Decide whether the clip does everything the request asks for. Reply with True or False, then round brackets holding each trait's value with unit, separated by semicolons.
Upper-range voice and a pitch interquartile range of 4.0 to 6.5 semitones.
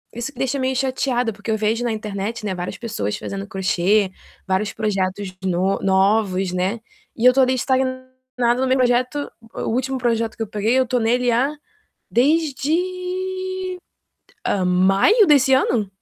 True (235 Hz; 4.9 semitones)